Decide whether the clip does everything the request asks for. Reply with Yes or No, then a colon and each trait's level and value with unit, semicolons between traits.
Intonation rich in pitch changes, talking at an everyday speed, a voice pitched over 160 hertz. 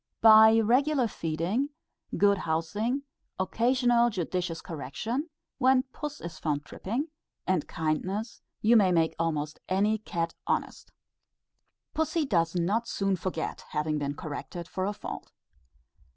No: wide, 6.1 semitones; slow, 125 wpm; high, 190 Hz